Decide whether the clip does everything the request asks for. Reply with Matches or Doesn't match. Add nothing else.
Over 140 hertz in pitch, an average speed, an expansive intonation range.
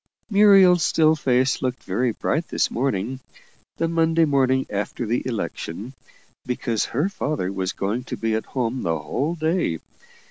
Doesn't match